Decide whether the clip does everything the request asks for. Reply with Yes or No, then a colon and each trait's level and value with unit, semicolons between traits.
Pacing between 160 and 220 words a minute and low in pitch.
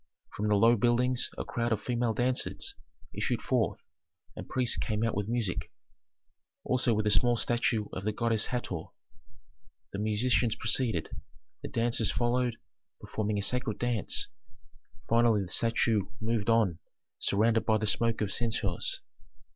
No: average, 145 wpm; low, 115 Hz